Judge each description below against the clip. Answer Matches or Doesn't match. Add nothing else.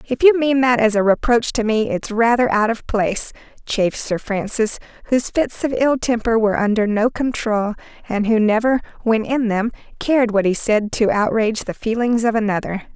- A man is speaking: Doesn't match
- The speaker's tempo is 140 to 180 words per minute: Doesn't match